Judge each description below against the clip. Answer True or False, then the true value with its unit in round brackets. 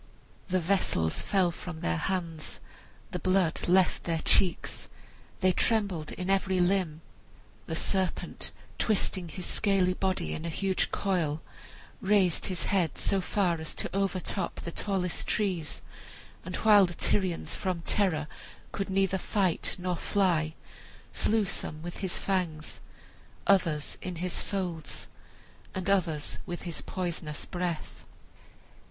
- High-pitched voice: False (180 Hz)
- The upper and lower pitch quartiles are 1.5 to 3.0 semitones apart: True (2.6 semitones)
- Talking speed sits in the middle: False (130 wpm)